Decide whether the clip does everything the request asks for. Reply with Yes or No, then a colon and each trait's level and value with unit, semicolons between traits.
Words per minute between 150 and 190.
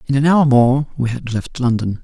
No: fast, 235 wpm